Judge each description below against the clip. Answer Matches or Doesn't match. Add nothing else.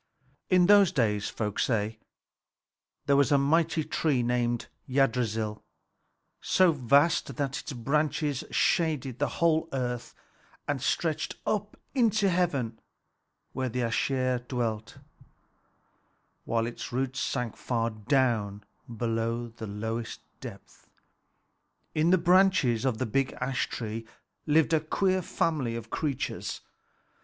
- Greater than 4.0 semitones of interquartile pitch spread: Matches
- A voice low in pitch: Matches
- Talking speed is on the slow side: Matches